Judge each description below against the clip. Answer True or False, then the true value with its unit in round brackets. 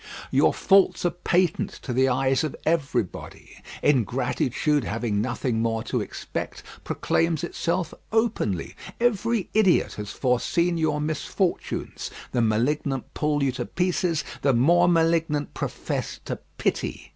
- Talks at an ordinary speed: False (125 wpm)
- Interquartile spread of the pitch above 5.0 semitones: True (5.6 semitones)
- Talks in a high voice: False (150 Hz)